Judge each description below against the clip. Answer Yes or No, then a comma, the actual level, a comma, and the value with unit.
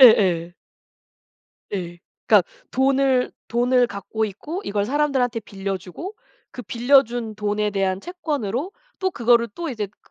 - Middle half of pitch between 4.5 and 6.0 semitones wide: Yes, average, 5.1 semitones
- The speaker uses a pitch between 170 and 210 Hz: No, high, 235 Hz